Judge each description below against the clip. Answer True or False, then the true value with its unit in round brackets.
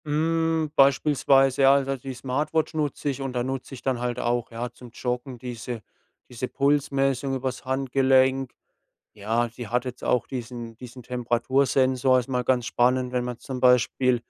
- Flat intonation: True (1.7 semitones)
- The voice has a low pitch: True (130 Hz)